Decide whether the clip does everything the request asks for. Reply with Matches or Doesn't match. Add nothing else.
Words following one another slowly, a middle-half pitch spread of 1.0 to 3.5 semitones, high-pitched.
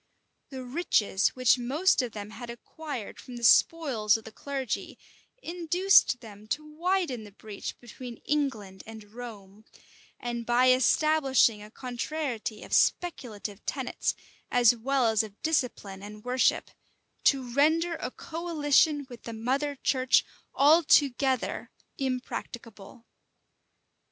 Doesn't match